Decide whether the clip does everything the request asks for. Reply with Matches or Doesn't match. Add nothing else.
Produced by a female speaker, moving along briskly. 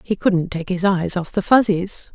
Matches